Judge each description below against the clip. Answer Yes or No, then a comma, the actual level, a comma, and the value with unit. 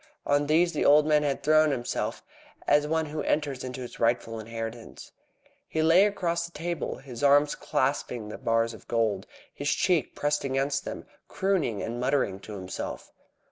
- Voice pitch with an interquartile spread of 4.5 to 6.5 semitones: Yes, average, 5.0 semitones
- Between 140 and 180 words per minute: Yes, average, 170 wpm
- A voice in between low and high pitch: Yes, medium, 145 Hz